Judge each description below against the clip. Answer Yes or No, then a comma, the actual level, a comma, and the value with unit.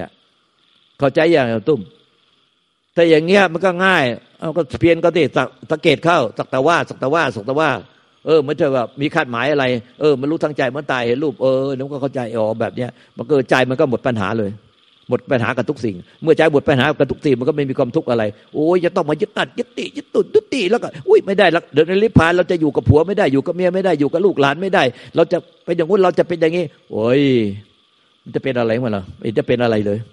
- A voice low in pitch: No, medium, 150 Hz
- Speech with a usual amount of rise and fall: No, wide, 5.7 semitones